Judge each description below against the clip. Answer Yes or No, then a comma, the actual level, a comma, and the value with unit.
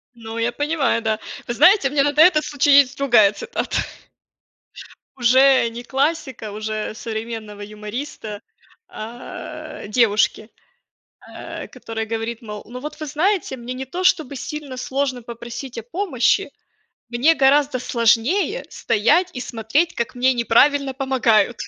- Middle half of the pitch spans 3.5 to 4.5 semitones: Yes, average, 4.1 semitones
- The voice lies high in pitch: Yes, very high, 250 Hz